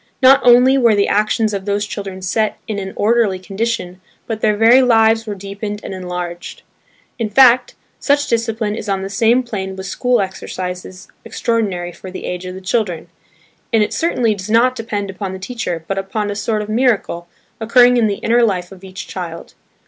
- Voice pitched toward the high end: Yes, high, 210 Hz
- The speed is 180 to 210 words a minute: Yes, average, 190 wpm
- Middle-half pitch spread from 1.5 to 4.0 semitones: Yes, average, 3.4 semitones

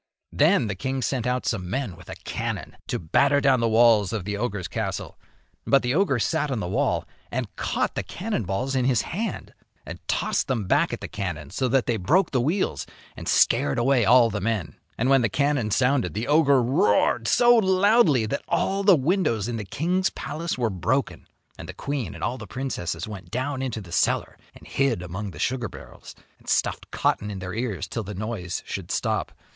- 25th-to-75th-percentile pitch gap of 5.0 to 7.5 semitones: Yes, average, 5.3 semitones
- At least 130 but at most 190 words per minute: No, fast, 205 wpm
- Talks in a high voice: No, low, 120 Hz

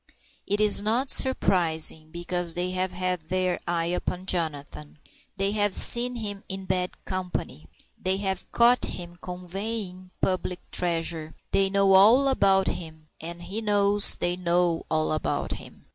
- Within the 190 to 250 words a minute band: No, average, 150 wpm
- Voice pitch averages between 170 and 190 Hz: Yes, medium, 185 Hz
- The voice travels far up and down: No, narrow, 2.6 semitones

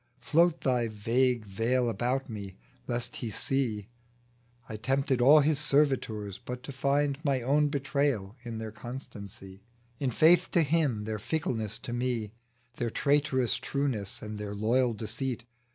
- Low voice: Yes, low, 125 Hz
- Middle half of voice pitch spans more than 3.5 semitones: Yes, average, 4.2 semitones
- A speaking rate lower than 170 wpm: Yes, average, 150 wpm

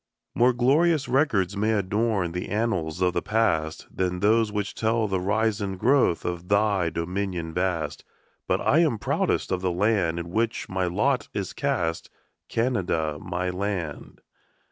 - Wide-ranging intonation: No, average, 4.1 semitones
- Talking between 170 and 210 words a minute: No, average, 155 wpm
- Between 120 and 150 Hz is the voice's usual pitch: No, very low, 95 Hz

